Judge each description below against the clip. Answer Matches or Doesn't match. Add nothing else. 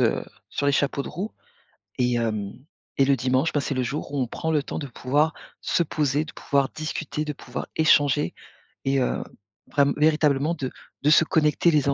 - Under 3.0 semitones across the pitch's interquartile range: Matches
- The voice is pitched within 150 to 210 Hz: Doesn't match